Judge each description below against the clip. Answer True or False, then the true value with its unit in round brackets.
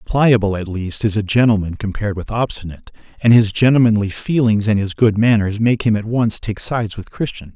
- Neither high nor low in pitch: False (110 Hz)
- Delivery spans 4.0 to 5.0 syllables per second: False (5.6 syllables/s)